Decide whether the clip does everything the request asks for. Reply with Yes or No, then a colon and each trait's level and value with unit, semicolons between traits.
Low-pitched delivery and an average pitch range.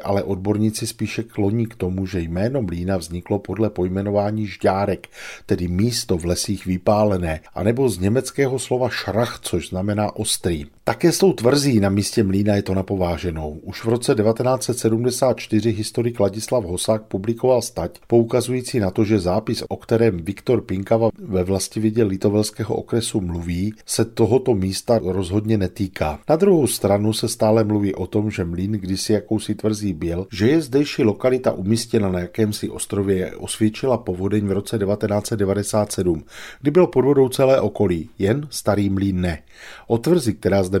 Yes: low, 105 Hz; average, 3.2 semitones